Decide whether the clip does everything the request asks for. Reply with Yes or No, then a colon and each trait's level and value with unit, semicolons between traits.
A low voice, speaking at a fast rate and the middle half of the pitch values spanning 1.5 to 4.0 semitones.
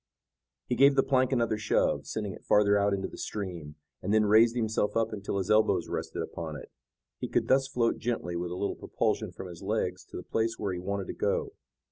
Yes: low, 105 Hz; fast, 220 wpm; average, 3.5 semitones